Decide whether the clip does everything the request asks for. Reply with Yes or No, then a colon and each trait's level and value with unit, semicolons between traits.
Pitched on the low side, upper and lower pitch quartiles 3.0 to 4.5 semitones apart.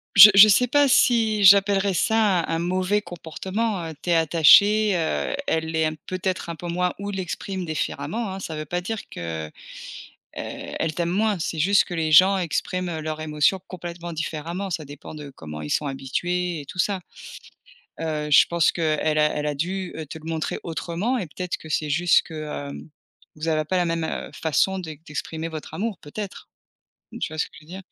No: medium, 170 Hz; average, 3.5 semitones